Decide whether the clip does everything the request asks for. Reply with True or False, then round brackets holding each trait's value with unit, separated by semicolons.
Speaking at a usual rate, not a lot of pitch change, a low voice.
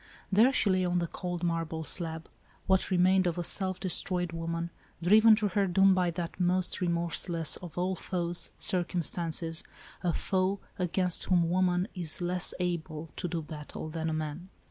False (165 wpm; 1.8 semitones; 175 Hz)